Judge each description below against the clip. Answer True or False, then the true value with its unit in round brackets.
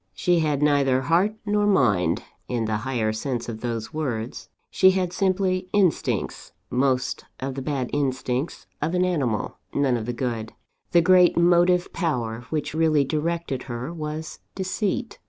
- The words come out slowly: False (155 wpm)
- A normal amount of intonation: False (6.1 semitones)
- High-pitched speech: False (145 Hz)